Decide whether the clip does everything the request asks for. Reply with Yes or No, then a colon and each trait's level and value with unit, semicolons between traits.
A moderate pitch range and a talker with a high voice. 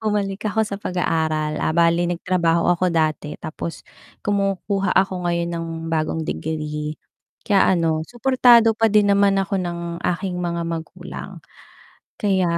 No: average, 3.3 semitones; medium, 180 Hz